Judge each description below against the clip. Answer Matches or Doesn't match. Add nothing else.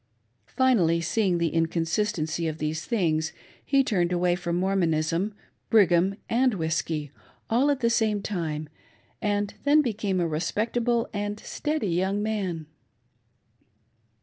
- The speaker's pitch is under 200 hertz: Matches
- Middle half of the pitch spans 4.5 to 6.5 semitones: Matches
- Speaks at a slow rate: Matches